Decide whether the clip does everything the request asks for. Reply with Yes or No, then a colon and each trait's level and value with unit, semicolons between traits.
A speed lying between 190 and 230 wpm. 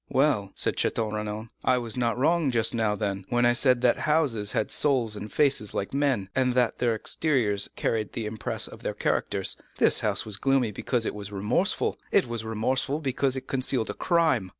Yes: average, 195 wpm